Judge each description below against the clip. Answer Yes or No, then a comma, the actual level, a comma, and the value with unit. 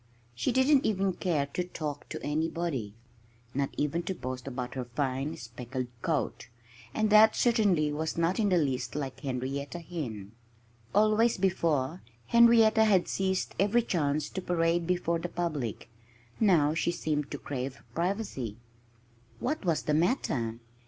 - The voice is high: No, medium, 165 Hz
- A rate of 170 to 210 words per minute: No, average, 145 wpm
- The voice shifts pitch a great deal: Yes, wide, 5.7 semitones